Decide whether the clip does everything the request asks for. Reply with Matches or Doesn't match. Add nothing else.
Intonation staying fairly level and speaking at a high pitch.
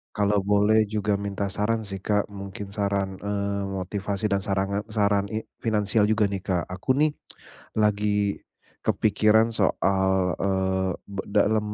Doesn't match